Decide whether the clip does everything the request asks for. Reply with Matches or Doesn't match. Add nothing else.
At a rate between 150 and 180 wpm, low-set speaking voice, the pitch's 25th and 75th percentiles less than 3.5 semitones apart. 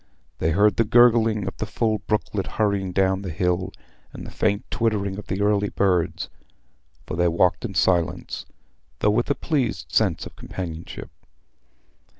Matches